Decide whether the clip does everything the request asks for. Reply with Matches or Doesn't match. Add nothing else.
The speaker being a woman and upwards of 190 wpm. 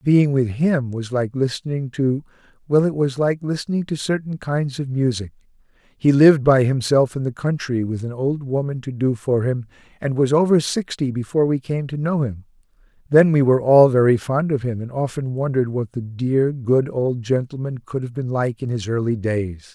Doesn't match